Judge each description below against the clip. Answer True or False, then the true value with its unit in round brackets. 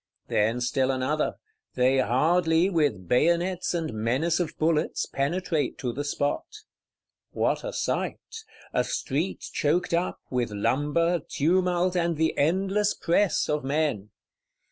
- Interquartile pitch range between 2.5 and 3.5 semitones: False (4.8 semitones)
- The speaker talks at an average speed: False (125 wpm)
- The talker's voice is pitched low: False (155 Hz)